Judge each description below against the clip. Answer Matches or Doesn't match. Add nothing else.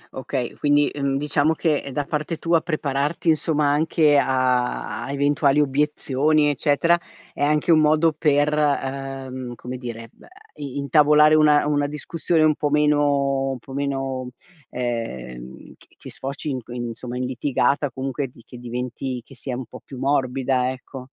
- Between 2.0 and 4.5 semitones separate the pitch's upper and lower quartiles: Matches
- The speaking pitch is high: Doesn't match